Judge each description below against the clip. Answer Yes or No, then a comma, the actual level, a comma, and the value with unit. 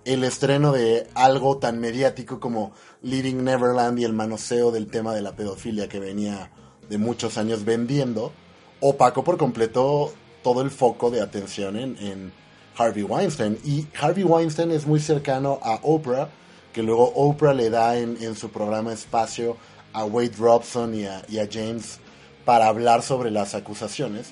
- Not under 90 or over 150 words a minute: No, average, 165 wpm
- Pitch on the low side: Yes, low, 115 Hz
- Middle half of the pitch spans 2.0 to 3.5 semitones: Yes, average, 3.2 semitones